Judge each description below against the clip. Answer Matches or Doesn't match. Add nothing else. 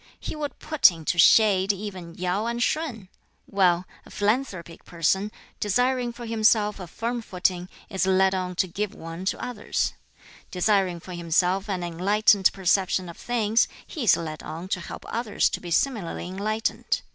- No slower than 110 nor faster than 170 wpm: Matches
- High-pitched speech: Matches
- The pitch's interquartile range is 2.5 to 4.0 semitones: Matches